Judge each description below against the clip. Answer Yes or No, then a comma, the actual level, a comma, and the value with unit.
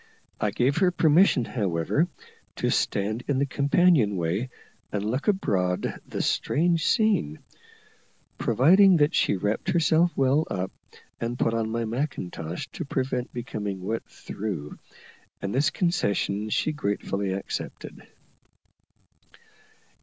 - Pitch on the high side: No, low, 120 Hz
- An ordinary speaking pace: No, slow, 125 wpm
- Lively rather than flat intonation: Yes, wide, 7.4 semitones